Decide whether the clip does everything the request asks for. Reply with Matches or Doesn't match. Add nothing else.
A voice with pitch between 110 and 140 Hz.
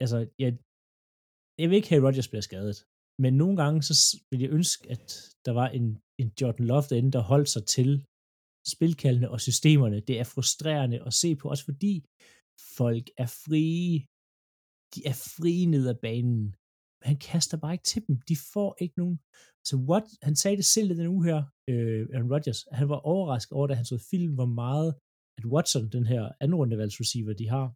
Matches